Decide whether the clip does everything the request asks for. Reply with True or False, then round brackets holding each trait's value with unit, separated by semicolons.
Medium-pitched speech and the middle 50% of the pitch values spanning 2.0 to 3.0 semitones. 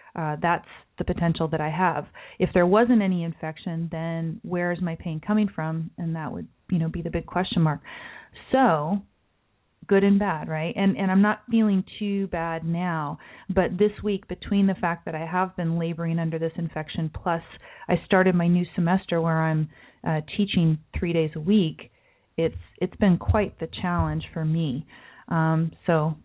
True (170 Hz; 2.6 semitones)